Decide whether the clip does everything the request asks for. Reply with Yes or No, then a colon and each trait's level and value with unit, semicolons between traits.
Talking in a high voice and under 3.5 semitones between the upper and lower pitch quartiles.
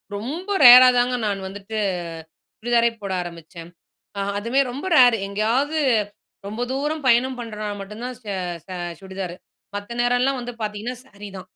No: high, 230 Hz; average, 3.8 semitones